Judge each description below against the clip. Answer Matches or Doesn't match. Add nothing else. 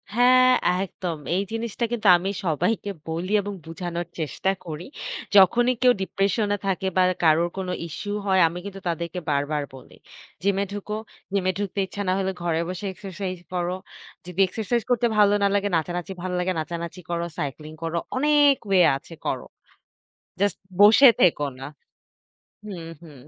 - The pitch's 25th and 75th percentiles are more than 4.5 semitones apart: Doesn't match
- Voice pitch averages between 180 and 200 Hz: Matches